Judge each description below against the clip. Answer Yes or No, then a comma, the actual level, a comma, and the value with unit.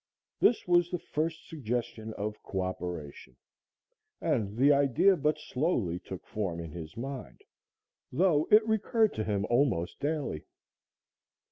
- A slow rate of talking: Yes, slow, 125 wpm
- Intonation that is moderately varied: No, wide, 8.7 semitones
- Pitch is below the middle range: Yes, low, 125 Hz